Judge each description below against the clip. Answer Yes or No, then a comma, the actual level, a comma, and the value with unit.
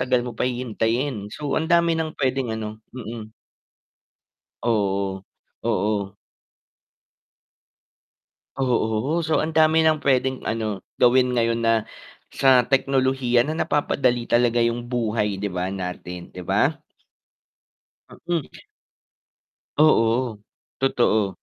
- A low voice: Yes, low, 120 Hz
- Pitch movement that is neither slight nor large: Yes, average, 3.7 semitones